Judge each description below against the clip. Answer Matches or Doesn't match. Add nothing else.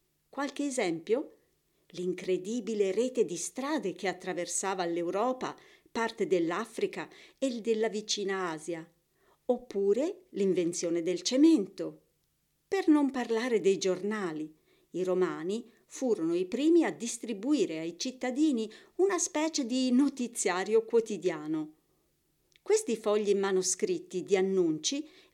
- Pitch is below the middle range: Doesn't match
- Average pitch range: Doesn't match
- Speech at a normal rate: Doesn't match